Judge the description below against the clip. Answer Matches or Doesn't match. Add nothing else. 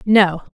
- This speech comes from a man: Doesn't match